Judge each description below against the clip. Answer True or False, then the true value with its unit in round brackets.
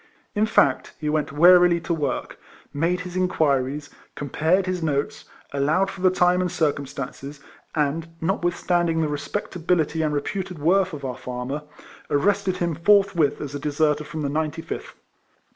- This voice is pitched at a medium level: True (160 Hz)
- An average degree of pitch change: True (3.8 semitones)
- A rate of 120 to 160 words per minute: True (155 wpm)